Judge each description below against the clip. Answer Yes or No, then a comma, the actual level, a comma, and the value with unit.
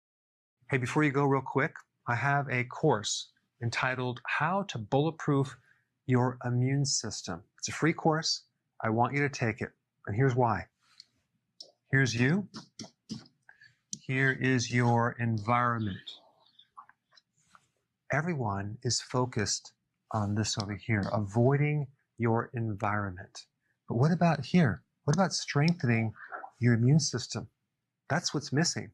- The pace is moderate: No, slow, 120 wpm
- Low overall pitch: Yes, low, 125 Hz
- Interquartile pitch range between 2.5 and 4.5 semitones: Yes, average, 3.5 semitones